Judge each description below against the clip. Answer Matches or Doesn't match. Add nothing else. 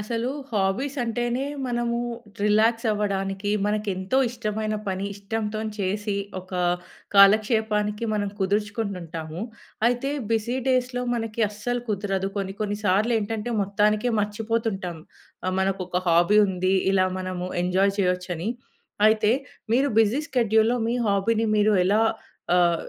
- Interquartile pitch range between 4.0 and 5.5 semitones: Doesn't match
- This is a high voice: Matches